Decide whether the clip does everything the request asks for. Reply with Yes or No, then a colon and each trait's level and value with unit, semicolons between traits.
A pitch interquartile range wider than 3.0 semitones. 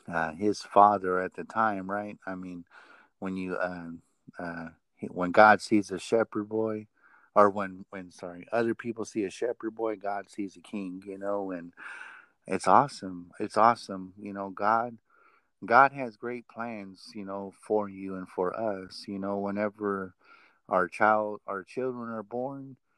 No: average, 2.7 semitones